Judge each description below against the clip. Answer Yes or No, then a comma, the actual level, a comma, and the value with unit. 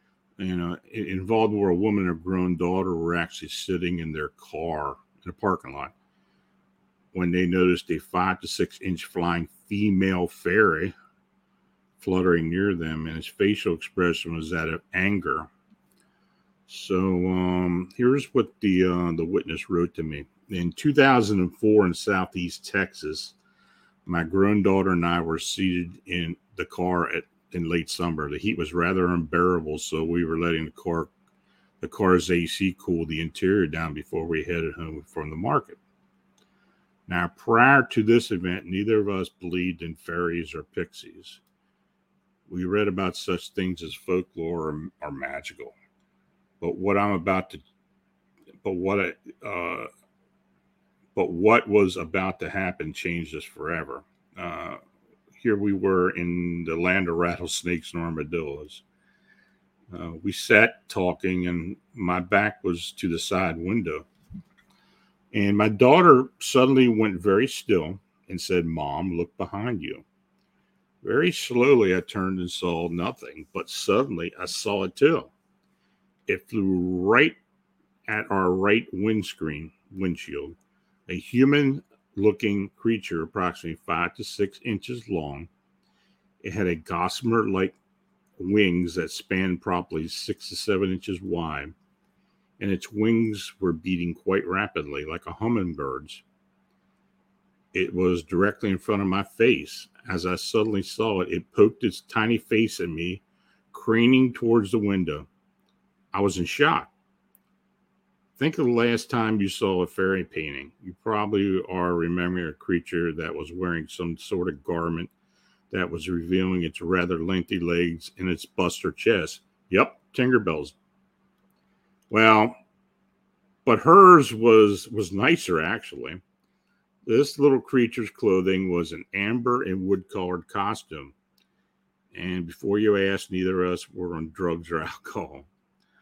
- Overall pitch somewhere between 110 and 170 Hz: No, very low, 90 Hz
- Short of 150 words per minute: Yes, average, 140 wpm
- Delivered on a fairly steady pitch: No, average, 3.5 semitones